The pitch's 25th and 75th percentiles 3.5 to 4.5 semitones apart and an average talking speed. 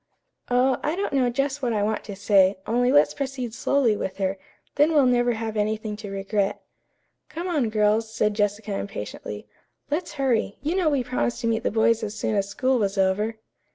Yes: average, 4.2 semitones; average, 195 wpm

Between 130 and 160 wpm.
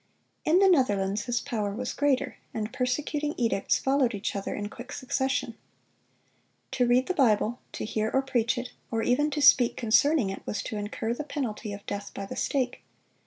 No: average, 185 wpm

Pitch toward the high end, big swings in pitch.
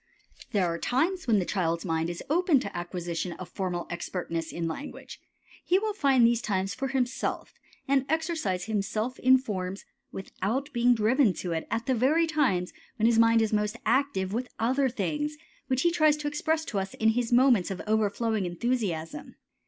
Yes: high, 230 Hz; wide, 6.2 semitones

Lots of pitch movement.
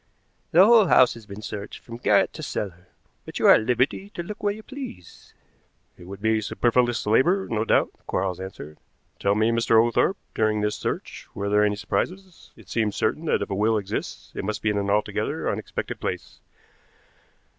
No: average, 4.2 semitones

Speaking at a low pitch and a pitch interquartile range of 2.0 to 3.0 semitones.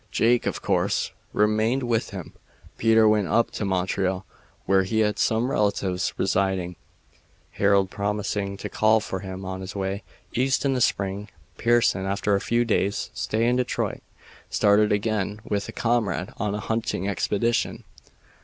Yes: low, 105 Hz; average, 2.7 semitones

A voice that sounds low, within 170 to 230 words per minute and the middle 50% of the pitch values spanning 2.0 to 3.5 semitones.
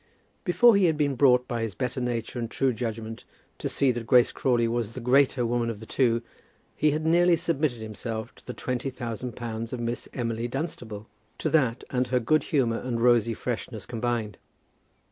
Yes: low, 120 Hz; average, 190 wpm; narrow, 2.6 semitones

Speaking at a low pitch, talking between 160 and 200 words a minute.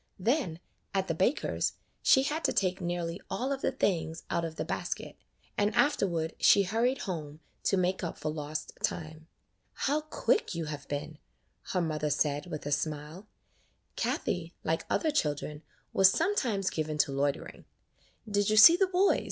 No: medium, 175 Hz; average, 165 wpm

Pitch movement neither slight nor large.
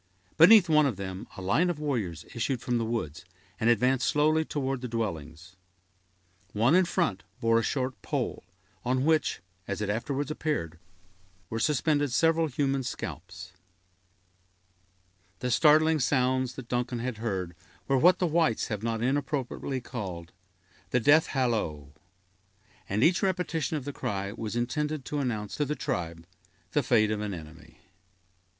No: wide, 6.0 semitones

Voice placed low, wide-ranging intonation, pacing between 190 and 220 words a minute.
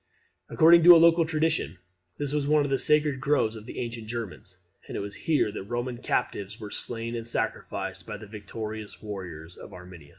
Yes: low, 115 Hz; wide, 6.3 semitones; average, 195 wpm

